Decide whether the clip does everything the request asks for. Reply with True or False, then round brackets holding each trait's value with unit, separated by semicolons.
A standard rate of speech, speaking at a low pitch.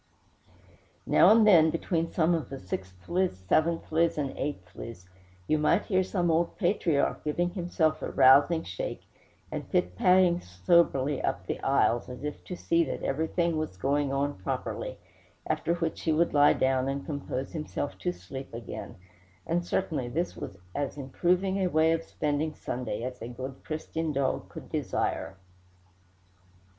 False (150 wpm; 155 Hz)